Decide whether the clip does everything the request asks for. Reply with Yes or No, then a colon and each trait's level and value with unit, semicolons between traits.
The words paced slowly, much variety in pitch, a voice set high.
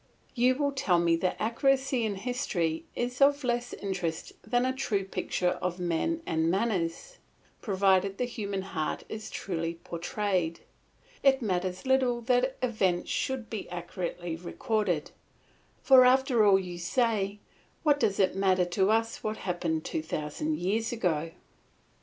No: average, 145 wpm; wide, 5.8 semitones; high, 200 Hz